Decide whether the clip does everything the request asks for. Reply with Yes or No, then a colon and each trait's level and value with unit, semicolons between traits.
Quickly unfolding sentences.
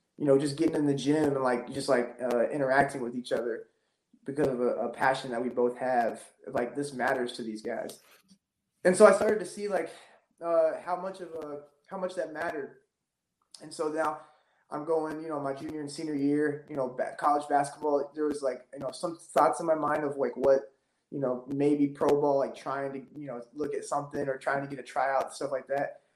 Yes: fast, 225 wpm